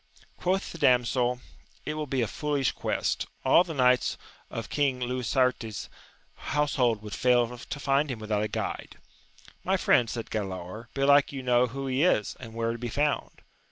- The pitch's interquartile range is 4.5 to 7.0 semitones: No, average, 3.4 semitones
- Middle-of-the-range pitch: No, low, 125 Hz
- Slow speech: No, average, 170 wpm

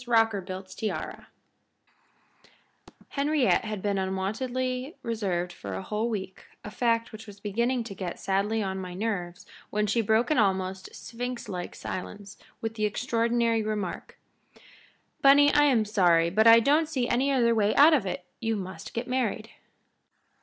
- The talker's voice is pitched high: Yes, high, 220 Hz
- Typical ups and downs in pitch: Yes, average, 3.9 semitones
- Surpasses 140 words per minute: Yes, average, 150 wpm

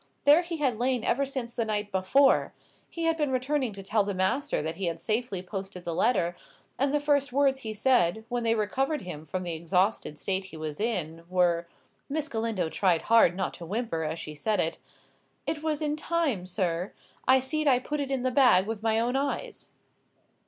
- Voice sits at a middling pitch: No, high, 225 Hz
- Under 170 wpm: No, average, 200 wpm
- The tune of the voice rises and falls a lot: Yes, wide, 6.8 semitones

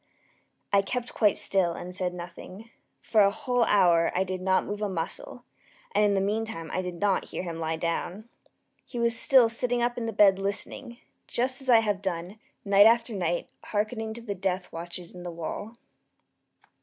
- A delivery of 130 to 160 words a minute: No, average, 190 wpm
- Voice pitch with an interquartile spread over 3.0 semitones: Yes, average, 4.1 semitones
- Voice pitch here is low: No, high, 200 Hz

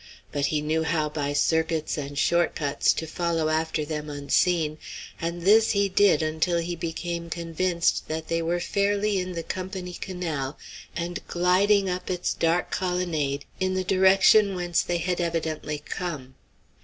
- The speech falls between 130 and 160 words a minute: Yes, average, 155 wpm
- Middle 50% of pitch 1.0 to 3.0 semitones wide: Yes, narrow, 2.6 semitones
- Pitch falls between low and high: Yes, medium, 170 Hz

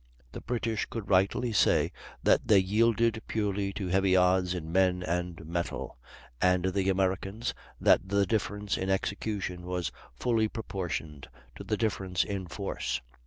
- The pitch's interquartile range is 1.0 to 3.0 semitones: Yes, narrow, 2.4 semitones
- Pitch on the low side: Yes, very low, 95 Hz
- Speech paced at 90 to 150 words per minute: Yes, average, 145 wpm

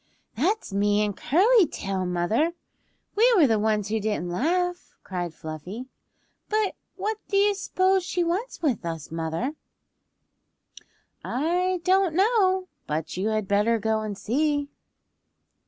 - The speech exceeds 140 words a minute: No, slow, 135 wpm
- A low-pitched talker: No, very high, 260 Hz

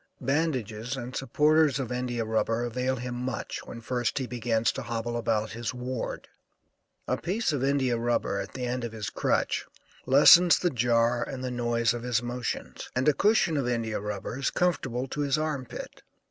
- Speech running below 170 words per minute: No, average, 185 wpm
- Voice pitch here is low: Yes, low, 125 Hz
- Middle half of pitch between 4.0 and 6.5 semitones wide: No, narrow, 2.4 semitones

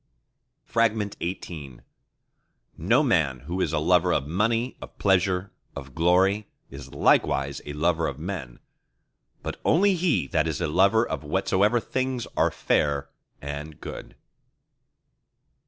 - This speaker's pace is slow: Yes, slow, 125 wpm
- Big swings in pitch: Yes, wide, 5.9 semitones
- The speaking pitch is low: Yes, very low, 90 Hz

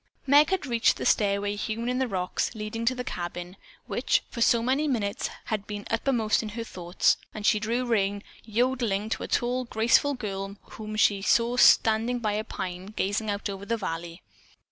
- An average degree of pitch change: Yes, average, 3.1 semitones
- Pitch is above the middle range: Yes, high, 220 Hz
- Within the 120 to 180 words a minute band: No, average, 190 wpm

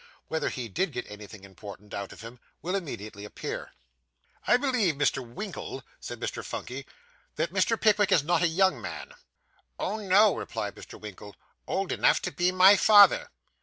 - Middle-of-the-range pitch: Yes, medium, 170 Hz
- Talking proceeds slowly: No, average, 165 wpm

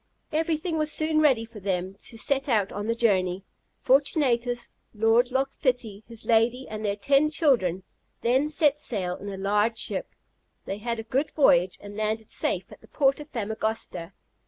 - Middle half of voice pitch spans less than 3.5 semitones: No, average, 5.0 semitones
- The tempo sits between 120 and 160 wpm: No, average, 175 wpm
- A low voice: No, high, 230 Hz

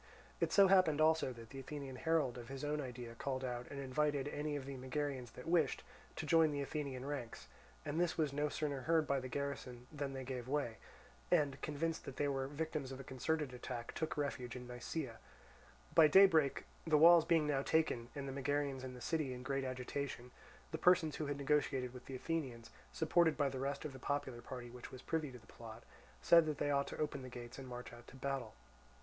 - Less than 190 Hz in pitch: Yes, medium, 140 Hz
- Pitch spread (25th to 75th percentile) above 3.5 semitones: No, average, 2.9 semitones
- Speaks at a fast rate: Yes, fast, 220 wpm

